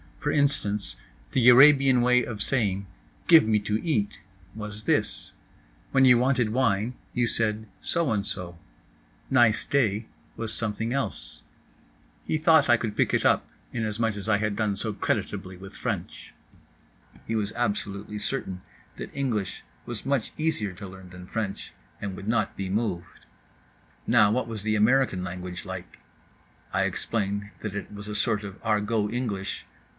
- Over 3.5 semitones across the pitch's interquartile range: No, average, 3.2 semitones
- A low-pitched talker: Yes, low, 110 Hz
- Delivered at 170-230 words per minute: No, average, 155 wpm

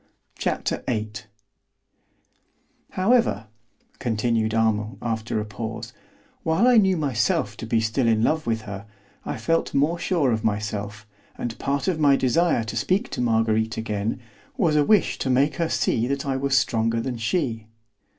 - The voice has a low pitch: Yes, low, 120 Hz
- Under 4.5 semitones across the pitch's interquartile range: No, average, 5.3 semitones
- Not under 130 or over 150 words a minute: No, average, 160 wpm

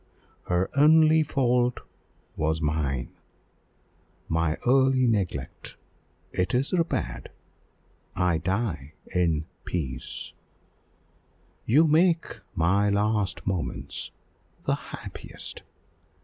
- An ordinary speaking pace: No, slow, 80 wpm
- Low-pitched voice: Yes, very low, 95 Hz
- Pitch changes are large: Yes, wide, 8.6 semitones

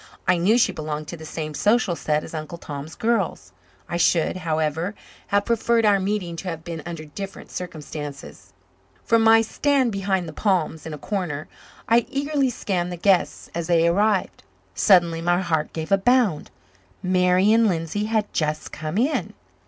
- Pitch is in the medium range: Yes, medium, 180 Hz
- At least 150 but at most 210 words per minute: Yes, average, 170 wpm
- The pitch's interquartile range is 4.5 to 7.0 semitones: Yes, average, 4.8 semitones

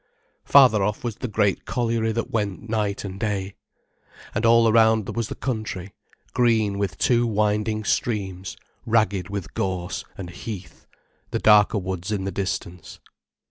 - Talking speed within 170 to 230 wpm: No, average, 145 wpm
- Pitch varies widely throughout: No, narrow, 2.6 semitones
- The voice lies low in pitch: Yes, low, 105 Hz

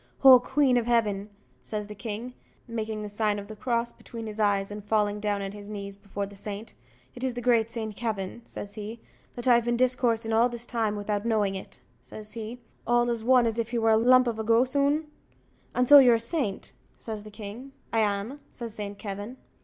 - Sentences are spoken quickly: Yes, fast, 215 wpm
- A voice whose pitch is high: Yes, high, 225 Hz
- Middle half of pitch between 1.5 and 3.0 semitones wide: Yes, narrow, 2.6 semitones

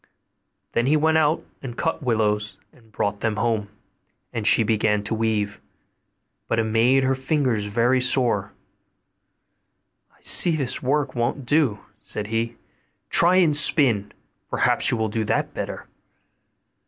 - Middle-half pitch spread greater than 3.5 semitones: Yes, average, 4.0 semitones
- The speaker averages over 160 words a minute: No, average, 140 wpm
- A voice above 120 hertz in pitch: No, low, 115 Hz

